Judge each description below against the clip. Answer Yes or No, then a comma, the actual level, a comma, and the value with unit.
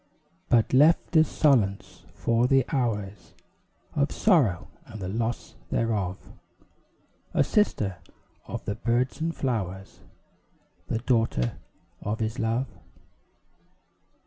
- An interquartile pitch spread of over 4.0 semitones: Yes, average, 4.7 semitones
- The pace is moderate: No, slow, 105 wpm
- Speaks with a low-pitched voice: Yes, low, 115 Hz